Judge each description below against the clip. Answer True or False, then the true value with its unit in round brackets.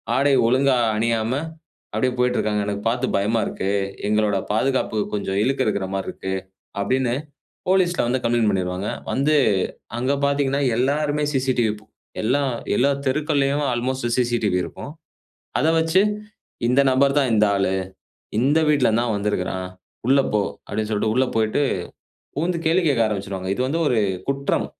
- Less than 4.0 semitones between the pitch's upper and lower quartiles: False (4.6 semitones)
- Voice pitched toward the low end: True (125 Hz)